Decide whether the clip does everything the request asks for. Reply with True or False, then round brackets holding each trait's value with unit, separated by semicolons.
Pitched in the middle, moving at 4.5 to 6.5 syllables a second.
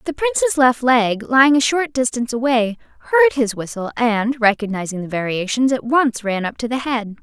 False (245 Hz; 5.4 syllables/s)